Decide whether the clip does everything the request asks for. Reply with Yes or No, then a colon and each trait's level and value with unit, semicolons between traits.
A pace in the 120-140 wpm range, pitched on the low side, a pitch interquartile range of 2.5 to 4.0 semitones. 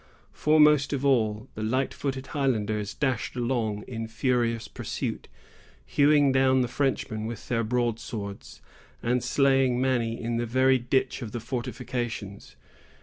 Yes: slow, 135 wpm; low, 120 Hz; average, 2.8 semitones